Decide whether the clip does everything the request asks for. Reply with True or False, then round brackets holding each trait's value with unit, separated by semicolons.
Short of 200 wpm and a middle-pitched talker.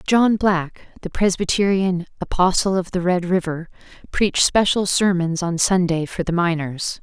True (145 wpm; 180 Hz)